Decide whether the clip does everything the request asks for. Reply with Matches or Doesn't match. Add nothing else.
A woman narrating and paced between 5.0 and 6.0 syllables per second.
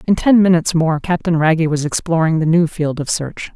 Matches